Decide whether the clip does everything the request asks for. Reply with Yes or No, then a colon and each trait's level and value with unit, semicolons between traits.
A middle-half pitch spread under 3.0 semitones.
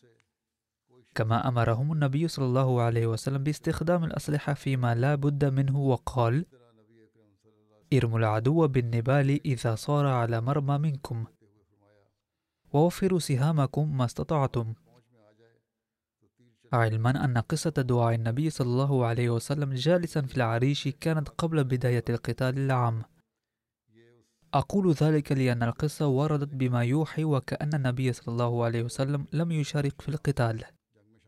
No: average, 3.9 semitones